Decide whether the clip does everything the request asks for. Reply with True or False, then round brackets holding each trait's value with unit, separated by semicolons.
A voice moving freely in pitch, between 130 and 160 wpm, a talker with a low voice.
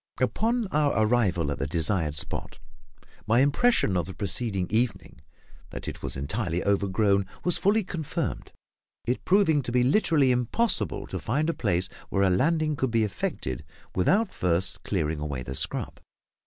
True (8.6 semitones; 155 wpm; 110 Hz)